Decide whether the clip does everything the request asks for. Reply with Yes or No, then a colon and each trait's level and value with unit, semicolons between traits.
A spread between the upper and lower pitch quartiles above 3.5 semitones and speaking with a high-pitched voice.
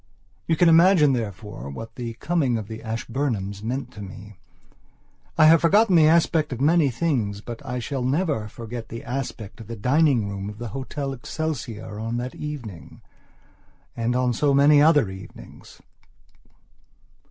No: average, 5.2 semitones; low, 125 Hz